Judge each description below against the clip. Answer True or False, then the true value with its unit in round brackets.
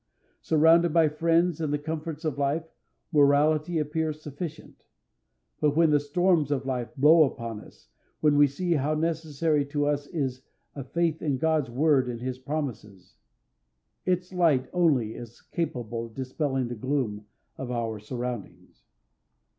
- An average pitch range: True (3.8 semitones)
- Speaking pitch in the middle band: True (145 Hz)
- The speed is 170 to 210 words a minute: False (145 wpm)